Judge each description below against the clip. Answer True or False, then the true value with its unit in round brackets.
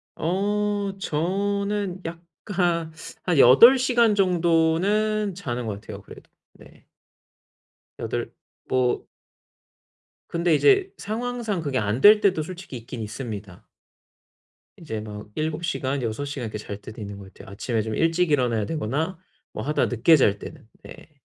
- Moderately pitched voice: True (160 Hz)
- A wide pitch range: True (8.7 semitones)